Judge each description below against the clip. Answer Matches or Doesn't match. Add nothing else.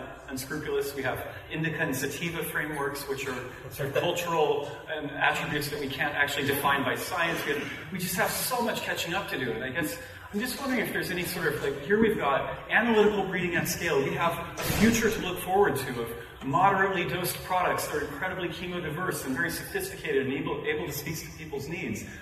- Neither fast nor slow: Doesn't match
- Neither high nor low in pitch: Matches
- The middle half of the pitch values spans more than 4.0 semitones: Matches